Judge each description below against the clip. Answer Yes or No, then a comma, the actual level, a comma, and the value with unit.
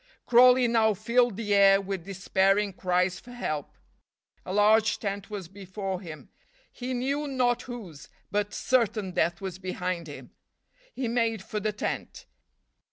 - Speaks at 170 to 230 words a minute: No, average, 145 wpm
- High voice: Yes, high, 205 Hz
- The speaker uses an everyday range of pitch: Yes, average, 3.8 semitones